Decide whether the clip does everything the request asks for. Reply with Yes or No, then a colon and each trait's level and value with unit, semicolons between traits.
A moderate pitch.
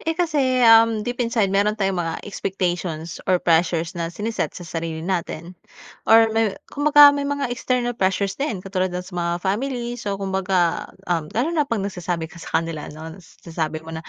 No: high, 195 Hz